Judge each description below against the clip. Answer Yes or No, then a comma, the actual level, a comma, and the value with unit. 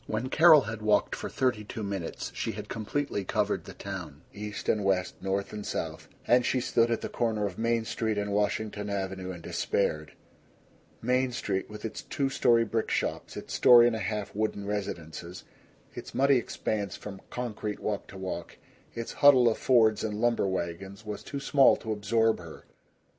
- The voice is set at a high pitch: No, low, 105 Hz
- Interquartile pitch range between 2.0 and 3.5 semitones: Yes, average, 2.9 semitones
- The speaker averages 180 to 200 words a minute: Yes, average, 185 wpm